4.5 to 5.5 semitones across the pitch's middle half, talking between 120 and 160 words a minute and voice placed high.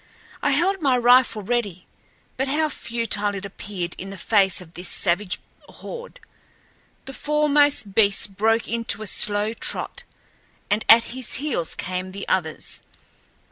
Yes: average, 5.1 semitones; average, 140 wpm; high, 220 Hz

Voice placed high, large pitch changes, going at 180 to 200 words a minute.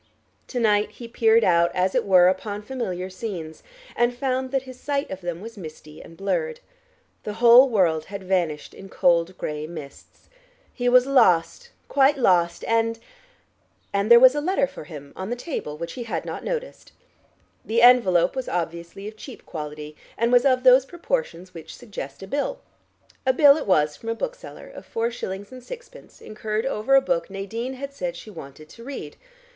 Yes: high, 220 Hz; wide, 6.6 semitones; average, 185 wpm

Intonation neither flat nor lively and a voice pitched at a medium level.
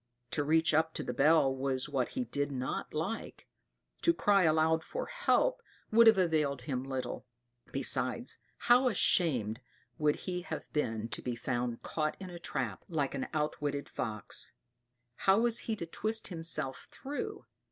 No: wide, 6.2 semitones; medium, 155 Hz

